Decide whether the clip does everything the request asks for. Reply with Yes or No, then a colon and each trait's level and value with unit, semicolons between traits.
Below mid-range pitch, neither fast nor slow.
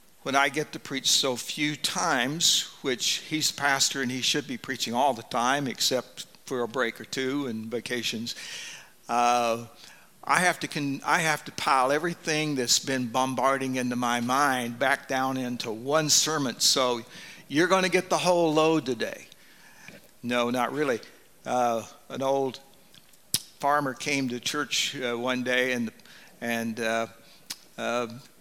Yes: low, 130 Hz; average, 160 wpm